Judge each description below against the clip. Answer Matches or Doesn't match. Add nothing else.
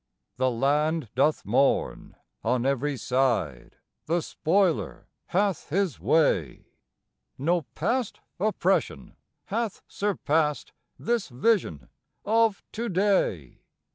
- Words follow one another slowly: Matches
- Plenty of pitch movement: Matches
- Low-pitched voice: Doesn't match